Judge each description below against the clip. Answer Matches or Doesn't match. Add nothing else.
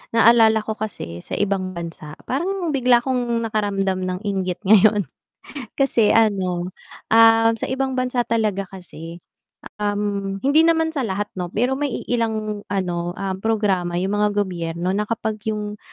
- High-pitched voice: Matches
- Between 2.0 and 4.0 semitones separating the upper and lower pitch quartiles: Matches